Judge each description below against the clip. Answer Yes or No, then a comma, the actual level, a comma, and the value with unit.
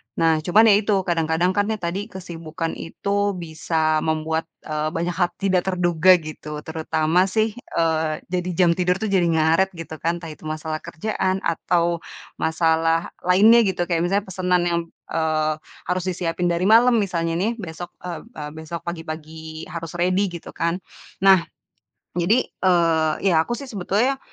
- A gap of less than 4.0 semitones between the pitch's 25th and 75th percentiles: Yes, average, 2.7 semitones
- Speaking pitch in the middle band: Yes, medium, 170 Hz